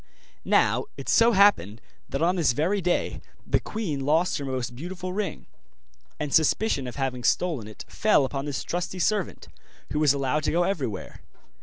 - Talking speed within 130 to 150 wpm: No, average, 170 wpm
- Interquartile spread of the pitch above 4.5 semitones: Yes, average, 5.3 semitones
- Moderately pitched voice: Yes, medium, 155 Hz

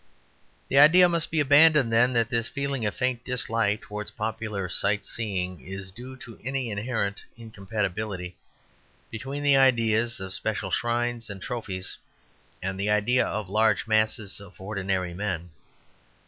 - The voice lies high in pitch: No, low, 110 Hz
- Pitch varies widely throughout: No, average, 3.8 semitones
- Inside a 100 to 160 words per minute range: Yes, average, 145 wpm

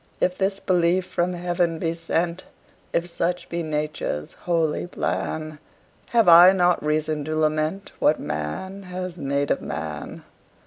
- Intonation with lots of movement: No, average, 2.7 semitones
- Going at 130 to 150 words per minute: Yes, average, 140 wpm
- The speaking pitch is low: No, medium, 170 Hz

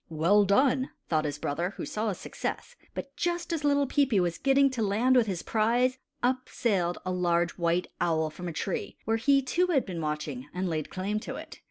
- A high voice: Yes, high, 205 Hz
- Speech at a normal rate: No, fast, 210 wpm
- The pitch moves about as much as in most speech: No, wide, 7.2 semitones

